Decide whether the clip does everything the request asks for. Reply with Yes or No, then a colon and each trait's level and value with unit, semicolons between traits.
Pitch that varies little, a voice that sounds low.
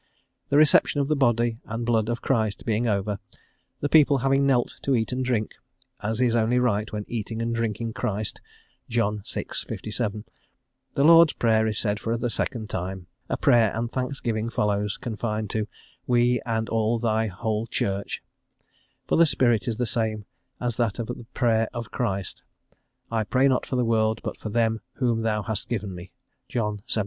Yes: narrow, 2.1 semitones; low, 115 Hz